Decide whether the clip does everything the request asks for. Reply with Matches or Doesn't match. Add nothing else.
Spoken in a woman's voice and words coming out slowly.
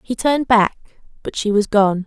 Doesn't match